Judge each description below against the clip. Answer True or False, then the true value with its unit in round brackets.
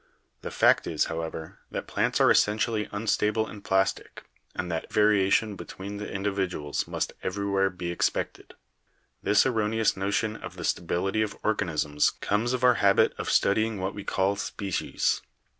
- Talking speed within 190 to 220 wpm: False (155 wpm)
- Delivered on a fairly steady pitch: True (2.1 semitones)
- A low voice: True (100 Hz)